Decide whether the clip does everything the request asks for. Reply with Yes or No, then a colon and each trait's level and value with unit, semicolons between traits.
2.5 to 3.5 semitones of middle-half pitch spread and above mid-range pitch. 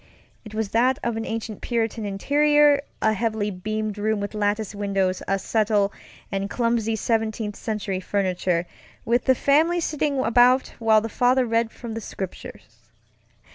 Yes: average, 2.8 semitones; high, 220 Hz